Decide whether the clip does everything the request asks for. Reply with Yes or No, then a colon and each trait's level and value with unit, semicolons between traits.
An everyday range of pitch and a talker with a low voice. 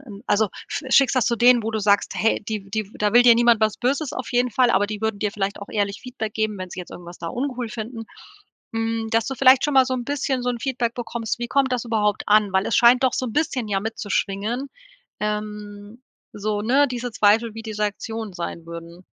No: average, 3.1 semitones; high, 225 Hz